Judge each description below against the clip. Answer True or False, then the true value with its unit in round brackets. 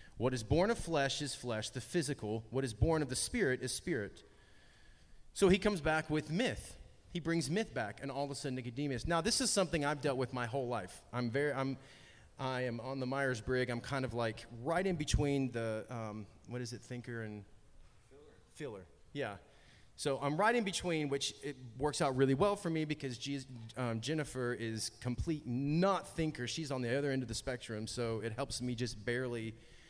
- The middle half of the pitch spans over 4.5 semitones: False (4.0 semitones)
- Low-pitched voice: True (130 Hz)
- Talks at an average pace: False (210 wpm)